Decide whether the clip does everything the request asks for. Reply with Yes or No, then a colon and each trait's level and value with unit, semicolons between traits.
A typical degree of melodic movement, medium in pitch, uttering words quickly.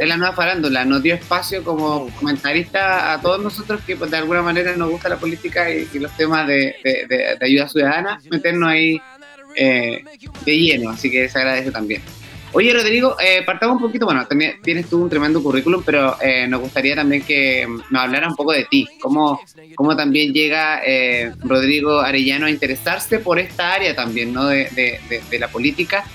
Yes: average, 4.5 semitones; medium, 155 Hz; fast, 195 wpm